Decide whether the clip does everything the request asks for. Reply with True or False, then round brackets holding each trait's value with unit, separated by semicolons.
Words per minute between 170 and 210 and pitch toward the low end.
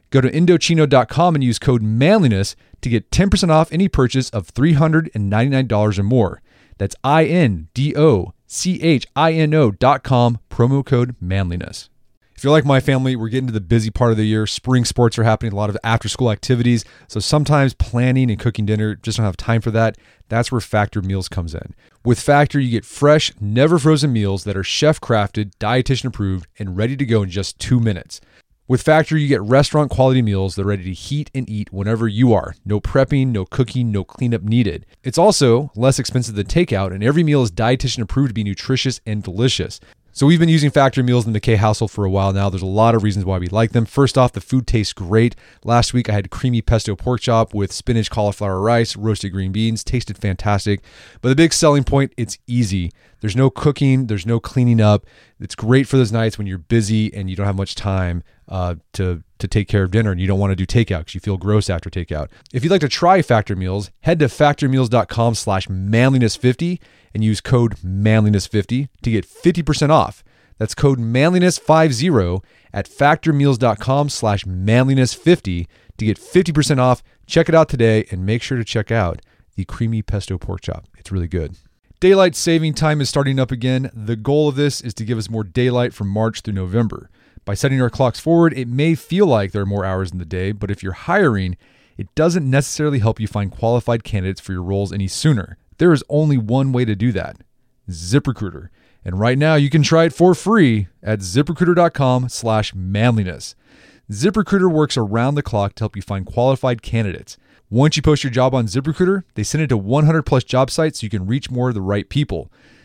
True (205 wpm; 115 Hz)